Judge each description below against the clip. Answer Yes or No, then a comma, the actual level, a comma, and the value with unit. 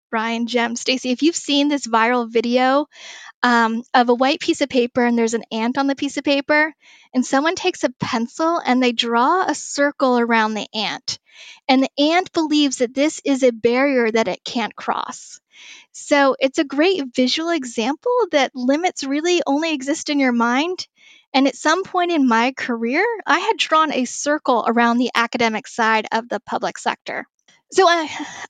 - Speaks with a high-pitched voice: Yes, very high, 270 Hz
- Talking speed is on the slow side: No, average, 185 wpm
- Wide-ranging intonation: No, average, 4.2 semitones